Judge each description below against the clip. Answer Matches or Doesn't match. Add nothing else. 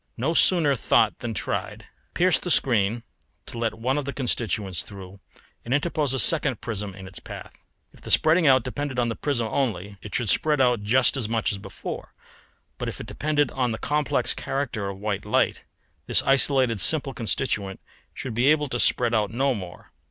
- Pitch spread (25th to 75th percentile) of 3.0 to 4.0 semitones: Doesn't match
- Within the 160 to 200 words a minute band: Matches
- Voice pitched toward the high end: Doesn't match